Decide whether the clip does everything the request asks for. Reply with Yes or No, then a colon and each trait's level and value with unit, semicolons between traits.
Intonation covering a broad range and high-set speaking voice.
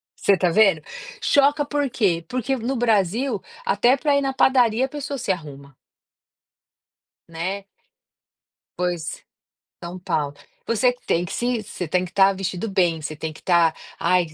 Yes: wide, 6.5 semitones; high, 195 Hz